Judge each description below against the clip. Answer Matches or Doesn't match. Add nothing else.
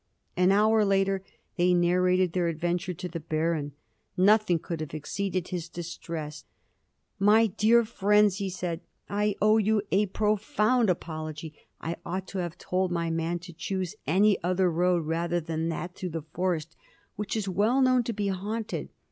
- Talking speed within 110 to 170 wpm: Matches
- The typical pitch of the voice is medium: Matches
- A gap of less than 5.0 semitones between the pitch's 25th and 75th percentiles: Matches